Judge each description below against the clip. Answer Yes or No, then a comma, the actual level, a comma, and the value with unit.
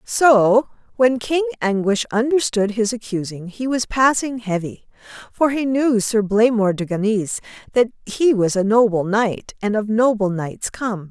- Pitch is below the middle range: No, high, 225 Hz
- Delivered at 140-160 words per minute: Yes, average, 155 wpm